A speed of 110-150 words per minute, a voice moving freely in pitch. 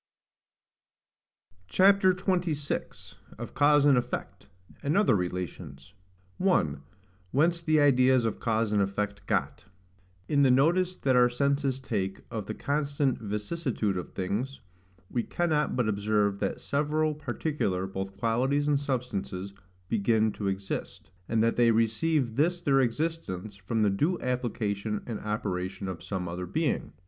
Yes: slow, 135 wpm; wide, 6.3 semitones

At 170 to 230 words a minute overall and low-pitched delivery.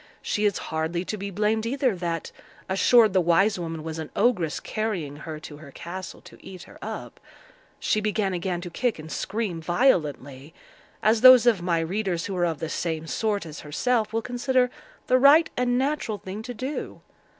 No: average, 185 wpm; high, 190 Hz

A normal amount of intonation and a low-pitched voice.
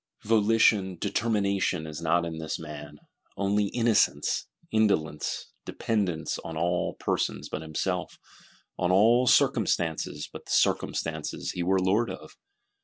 Yes: average, 4.6 semitones; very low, 90 Hz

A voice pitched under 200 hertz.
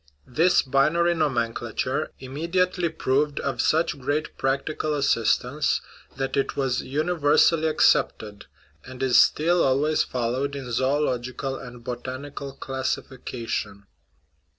Yes: low, 135 Hz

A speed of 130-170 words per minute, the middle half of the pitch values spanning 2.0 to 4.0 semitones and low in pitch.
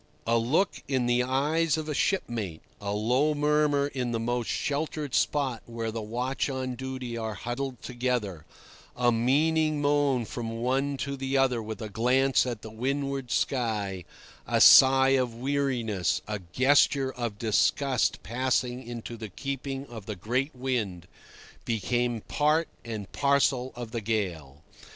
Yes: average, 150 wpm; average, 3.3 semitones; low, 125 Hz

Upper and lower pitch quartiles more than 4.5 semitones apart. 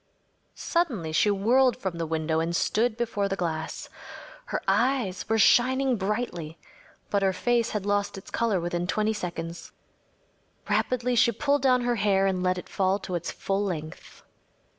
Yes: average, 5.2 semitones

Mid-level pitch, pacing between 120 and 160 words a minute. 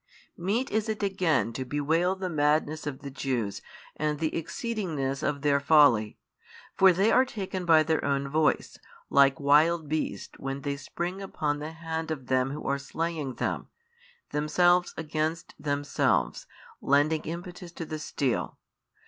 Yes: medium, 155 Hz; average, 150 wpm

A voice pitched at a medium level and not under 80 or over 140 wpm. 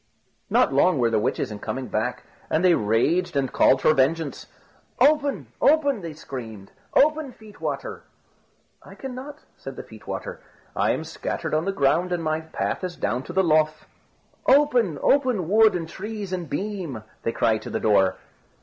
No: medium, 170 Hz; average, 175 wpm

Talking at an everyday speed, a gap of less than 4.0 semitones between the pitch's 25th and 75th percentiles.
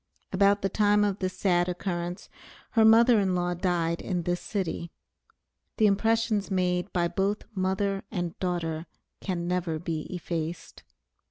Yes: average, 145 wpm; narrow, 2.5 semitones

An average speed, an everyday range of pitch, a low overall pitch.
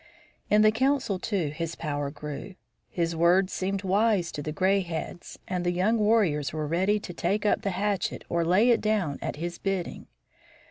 No: average, 185 wpm; average, 3.7 semitones; medium, 185 Hz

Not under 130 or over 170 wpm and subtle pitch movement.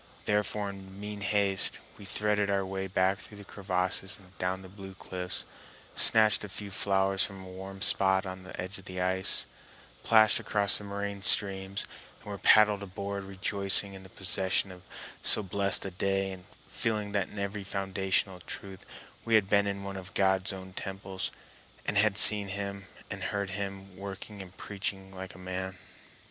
No: average, 180 wpm; narrow, 1.1 semitones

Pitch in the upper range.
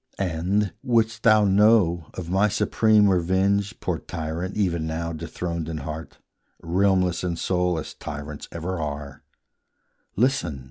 No: very low, 90 Hz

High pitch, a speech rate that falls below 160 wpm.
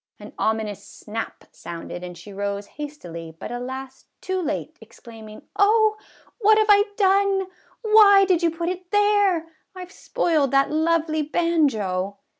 Yes: very high, 315 Hz; average, 150 wpm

